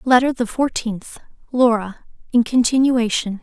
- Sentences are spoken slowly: Yes, slow, 105 wpm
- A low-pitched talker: No, high, 235 Hz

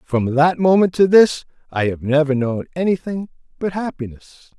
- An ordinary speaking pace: Yes, average, 155 wpm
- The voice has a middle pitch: Yes, medium, 160 Hz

